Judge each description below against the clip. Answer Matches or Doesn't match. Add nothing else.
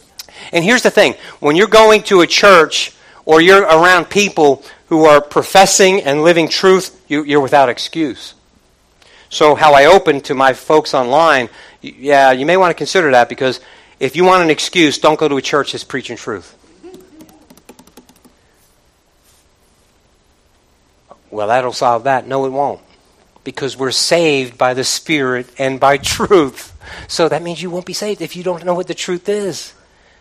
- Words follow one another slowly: Doesn't match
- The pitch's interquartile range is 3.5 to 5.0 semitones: Doesn't match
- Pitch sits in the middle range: Matches